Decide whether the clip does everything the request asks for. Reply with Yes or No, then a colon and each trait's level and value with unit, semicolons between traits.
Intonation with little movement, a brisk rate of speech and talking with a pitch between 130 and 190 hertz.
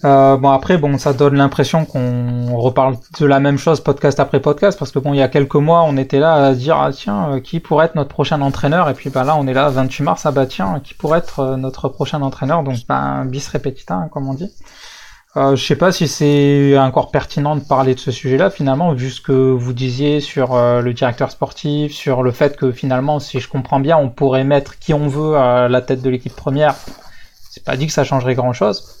Yes: narrow, 2.2 semitones; fast, 245 wpm; medium, 140 Hz